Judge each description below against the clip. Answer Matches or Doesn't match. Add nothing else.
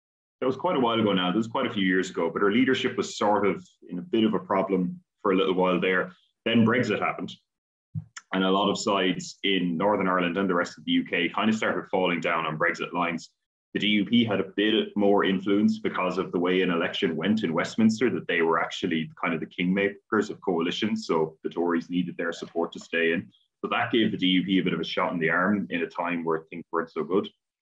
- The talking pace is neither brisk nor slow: Doesn't match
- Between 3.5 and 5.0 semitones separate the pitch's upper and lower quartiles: Doesn't match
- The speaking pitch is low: Matches